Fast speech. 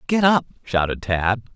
No: average, 155 wpm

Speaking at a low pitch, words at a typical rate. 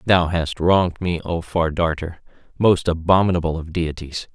Yes: very low, 85 Hz; average, 150 wpm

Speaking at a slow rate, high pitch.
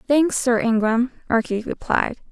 Yes: slow, 130 wpm; high, 240 Hz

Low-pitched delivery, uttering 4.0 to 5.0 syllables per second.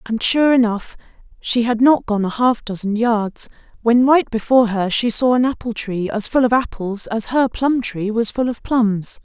No: high, 230 Hz; 4.6 syllables/s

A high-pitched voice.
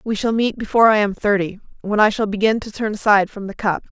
Yes: high, 210 Hz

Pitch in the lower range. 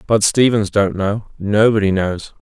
Yes: low, 105 Hz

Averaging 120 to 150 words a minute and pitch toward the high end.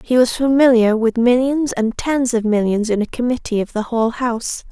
No: fast, 205 wpm; high, 240 Hz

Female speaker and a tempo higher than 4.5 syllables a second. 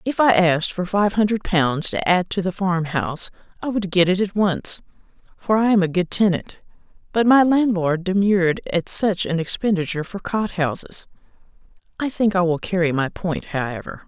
Yes: female; 5.0 syllables/s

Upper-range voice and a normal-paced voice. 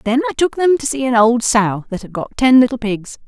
No: high, 240 Hz; fast, 275 wpm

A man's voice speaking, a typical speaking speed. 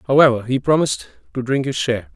Yes: male; average, 195 wpm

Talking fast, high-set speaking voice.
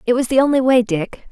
Yes: fast, 275 wpm; high, 245 Hz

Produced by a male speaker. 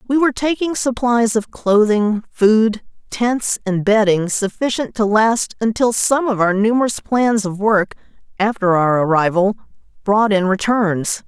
No: female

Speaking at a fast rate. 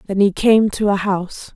Yes: fast, 230 wpm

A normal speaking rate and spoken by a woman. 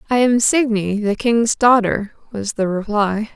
Yes: average, 160 wpm; female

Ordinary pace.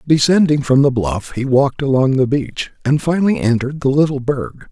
Yes: average, 190 wpm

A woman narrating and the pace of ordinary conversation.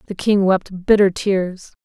Yes: female; average, 165 wpm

